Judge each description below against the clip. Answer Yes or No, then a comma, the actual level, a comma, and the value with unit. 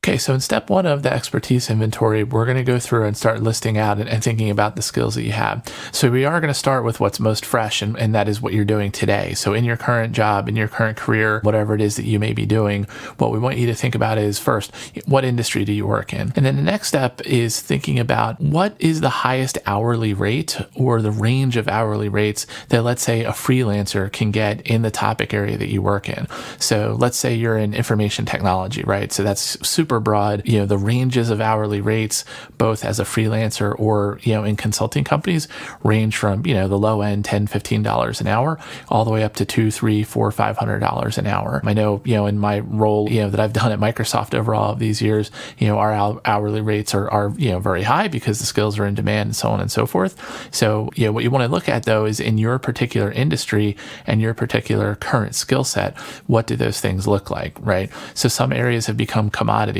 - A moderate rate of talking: No, fast, 240 wpm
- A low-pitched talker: Yes, low, 110 Hz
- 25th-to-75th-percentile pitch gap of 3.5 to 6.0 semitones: No, narrow, 2.5 semitones